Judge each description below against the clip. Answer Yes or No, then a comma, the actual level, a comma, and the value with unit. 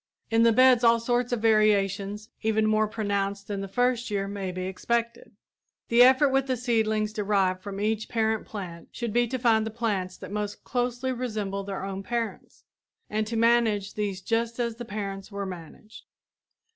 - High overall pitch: Yes, high, 215 Hz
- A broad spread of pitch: No, average, 2.8 semitones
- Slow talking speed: No, average, 180 wpm